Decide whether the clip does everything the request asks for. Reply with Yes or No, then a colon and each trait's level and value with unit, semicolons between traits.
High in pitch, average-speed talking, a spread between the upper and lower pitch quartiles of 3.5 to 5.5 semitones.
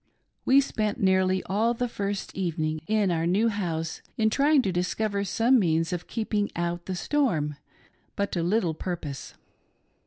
Yes: high, 195 Hz; average, 155 wpm; average, 4.2 semitones